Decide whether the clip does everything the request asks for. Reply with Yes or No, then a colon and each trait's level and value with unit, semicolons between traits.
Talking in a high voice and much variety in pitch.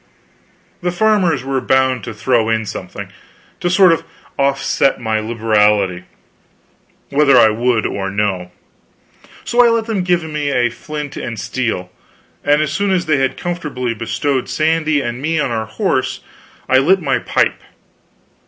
No: low, 135 Hz; wide, 5.9 semitones